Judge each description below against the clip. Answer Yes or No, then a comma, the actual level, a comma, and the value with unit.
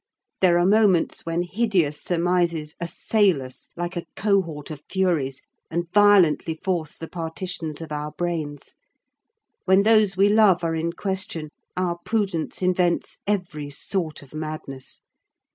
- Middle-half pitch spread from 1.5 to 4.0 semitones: Yes, average, 3.5 semitones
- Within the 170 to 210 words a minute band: No, slow, 135 wpm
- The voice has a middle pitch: Yes, medium, 175 Hz